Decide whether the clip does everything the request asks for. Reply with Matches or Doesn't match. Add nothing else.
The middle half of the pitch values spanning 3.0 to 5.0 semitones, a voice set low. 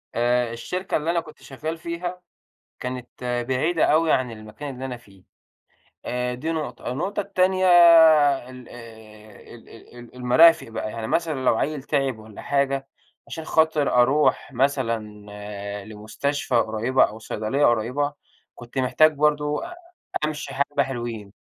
Matches